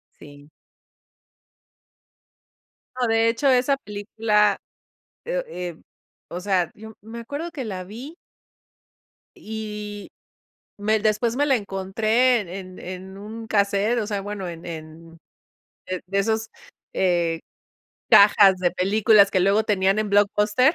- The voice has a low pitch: No, high, 205 Hz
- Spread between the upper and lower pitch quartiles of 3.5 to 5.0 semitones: No, average, 3.0 semitones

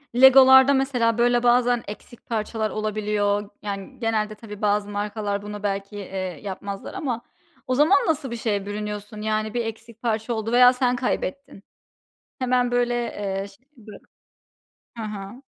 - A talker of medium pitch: No, high, 220 Hz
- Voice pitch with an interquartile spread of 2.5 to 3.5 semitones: Yes, average, 3.0 semitones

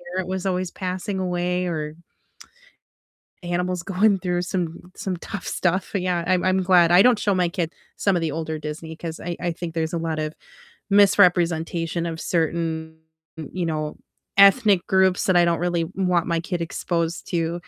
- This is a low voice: No, medium, 175 Hz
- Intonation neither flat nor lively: No, narrow, 2.0 semitones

